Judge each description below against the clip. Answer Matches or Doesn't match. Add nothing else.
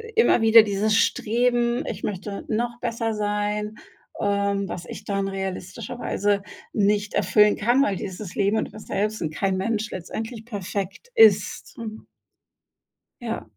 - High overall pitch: Matches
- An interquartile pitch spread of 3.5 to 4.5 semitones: Doesn't match